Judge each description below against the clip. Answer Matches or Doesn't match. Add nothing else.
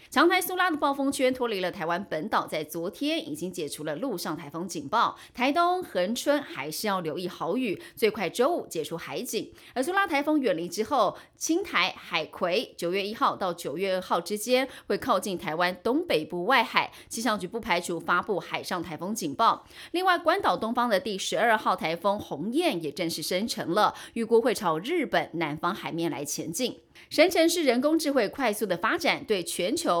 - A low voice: Doesn't match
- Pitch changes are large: Matches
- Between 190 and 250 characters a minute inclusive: Doesn't match